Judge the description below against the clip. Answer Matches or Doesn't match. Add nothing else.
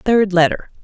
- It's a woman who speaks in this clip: Matches